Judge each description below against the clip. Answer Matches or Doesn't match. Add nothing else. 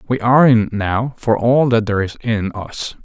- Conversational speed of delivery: Doesn't match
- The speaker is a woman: Doesn't match